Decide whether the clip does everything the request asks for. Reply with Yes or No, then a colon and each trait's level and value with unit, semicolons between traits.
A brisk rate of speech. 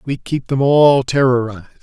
No: average, 165 wpm